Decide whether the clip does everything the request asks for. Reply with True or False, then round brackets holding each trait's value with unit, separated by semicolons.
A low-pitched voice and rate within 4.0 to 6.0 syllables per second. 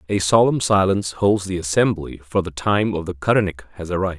False (95 Hz; 6.4 syllables/s)